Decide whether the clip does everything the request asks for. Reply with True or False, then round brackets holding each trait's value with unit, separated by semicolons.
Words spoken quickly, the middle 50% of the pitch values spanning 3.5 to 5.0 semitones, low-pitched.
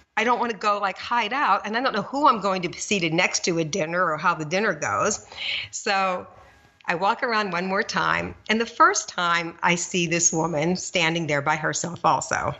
False (225 wpm; 3.8 semitones; 190 Hz)